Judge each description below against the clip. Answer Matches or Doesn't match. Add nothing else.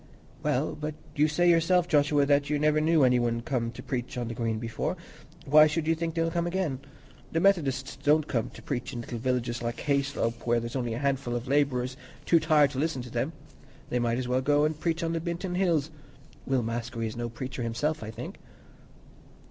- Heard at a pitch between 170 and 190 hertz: Doesn't match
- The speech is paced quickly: Matches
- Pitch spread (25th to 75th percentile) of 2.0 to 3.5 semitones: Doesn't match